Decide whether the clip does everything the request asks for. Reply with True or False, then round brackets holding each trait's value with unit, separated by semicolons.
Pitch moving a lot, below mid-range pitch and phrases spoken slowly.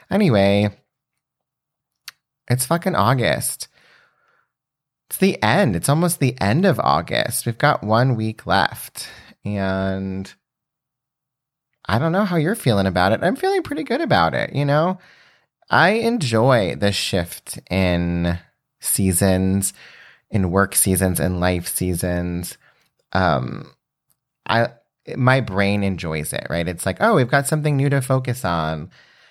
True (7.0 semitones; 105 Hz; 130 wpm)